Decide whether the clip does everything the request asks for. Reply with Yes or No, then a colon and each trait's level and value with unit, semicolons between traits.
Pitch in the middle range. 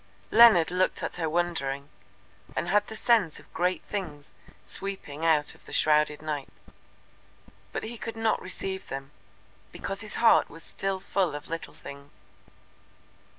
Yes: medium, 175 Hz